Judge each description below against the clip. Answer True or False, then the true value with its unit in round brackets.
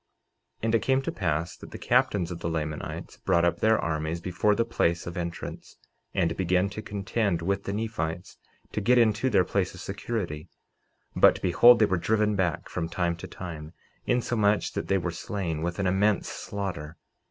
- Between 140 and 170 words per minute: False (185 wpm)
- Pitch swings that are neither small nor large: True (3.9 semitones)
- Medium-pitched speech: False (95 Hz)